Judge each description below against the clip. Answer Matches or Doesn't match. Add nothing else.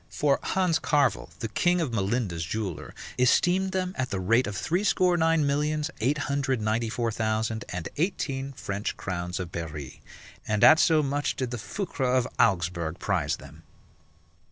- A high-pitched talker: Doesn't match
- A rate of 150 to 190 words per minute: Matches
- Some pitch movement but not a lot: Doesn't match